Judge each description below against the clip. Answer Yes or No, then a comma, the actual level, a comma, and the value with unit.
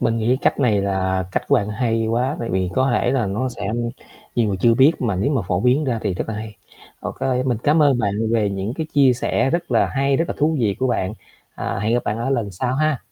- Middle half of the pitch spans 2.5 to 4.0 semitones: No, average, 4.5 semitones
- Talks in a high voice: No, low, 115 Hz